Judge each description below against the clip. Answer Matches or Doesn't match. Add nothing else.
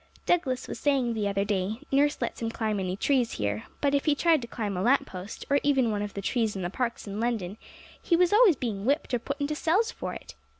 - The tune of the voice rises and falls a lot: Matches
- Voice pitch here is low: Doesn't match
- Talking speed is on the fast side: Matches